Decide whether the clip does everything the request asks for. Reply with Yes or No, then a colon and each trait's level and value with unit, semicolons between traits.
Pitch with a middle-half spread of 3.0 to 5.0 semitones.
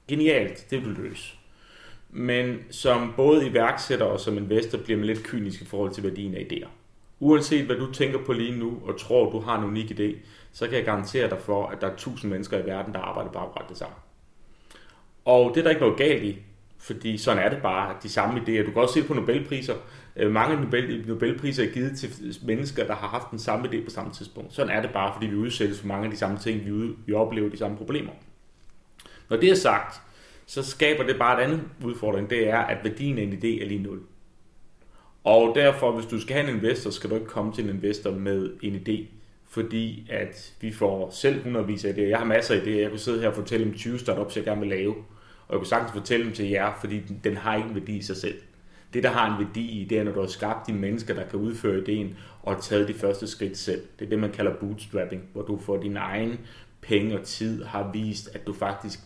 No: narrow, 2.5 semitones